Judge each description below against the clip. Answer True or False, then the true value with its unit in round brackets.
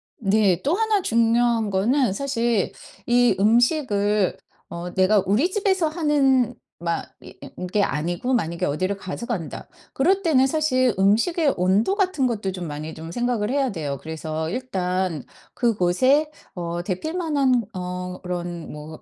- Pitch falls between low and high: False (210 Hz)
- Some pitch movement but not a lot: False (6.7 semitones)